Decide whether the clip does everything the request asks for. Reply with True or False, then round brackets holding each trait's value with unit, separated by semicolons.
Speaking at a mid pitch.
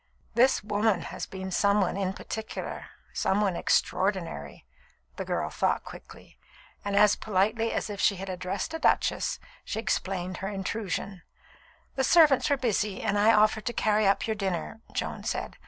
False (205 Hz)